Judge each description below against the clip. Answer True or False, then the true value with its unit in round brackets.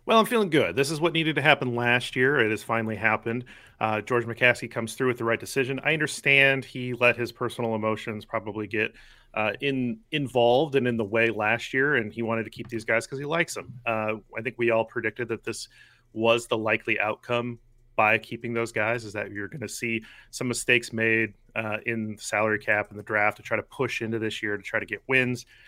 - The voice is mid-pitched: False (115 Hz)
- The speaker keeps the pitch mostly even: True (2.1 semitones)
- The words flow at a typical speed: False (230 wpm)